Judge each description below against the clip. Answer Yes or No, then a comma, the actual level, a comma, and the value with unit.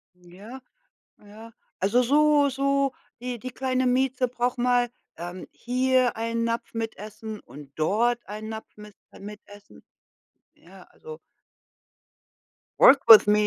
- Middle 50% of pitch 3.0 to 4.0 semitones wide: Yes, average, 3.4 semitones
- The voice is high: Yes, high, 235 Hz